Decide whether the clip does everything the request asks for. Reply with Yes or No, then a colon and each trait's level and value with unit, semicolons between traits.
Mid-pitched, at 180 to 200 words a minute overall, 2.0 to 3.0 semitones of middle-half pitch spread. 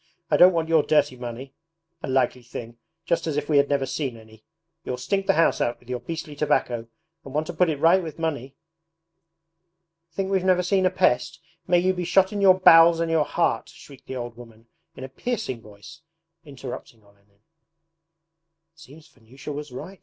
No: medium, 150 Hz; average, 195 wpm; average, 4.8 semitones